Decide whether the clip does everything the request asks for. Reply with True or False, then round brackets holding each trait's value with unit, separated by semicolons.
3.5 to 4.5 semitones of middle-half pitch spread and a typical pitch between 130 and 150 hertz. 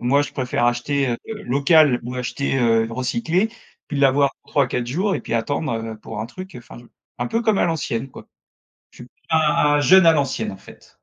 True (4.2 semitones; 135 Hz)